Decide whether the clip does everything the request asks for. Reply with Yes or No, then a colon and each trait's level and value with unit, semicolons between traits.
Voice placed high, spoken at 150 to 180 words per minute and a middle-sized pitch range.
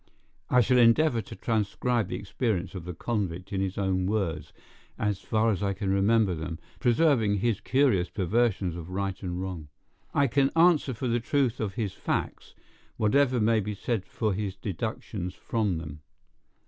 No: low, 105 Hz; average, 170 wpm; average, 4.1 semitones